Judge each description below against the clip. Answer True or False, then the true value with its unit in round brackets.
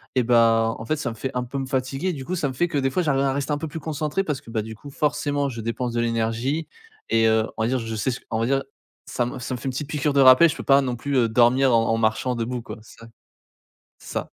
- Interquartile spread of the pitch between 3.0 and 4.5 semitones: True (3.7 semitones)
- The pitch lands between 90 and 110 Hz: False (130 Hz)